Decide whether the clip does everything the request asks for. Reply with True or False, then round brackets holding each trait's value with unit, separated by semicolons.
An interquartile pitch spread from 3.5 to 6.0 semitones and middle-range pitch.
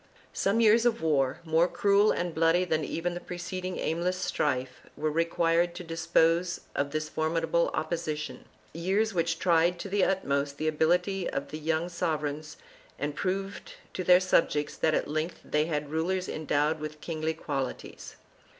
False (2.6 semitones; 165 Hz)